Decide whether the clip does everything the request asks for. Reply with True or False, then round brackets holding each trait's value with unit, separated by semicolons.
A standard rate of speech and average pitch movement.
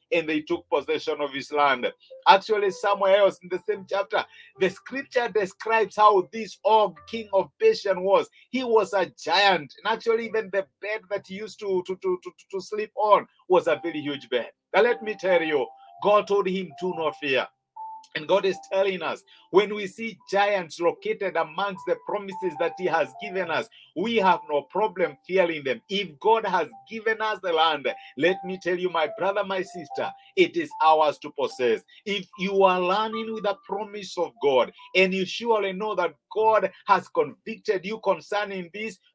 True (190 wpm; 3.7 semitones)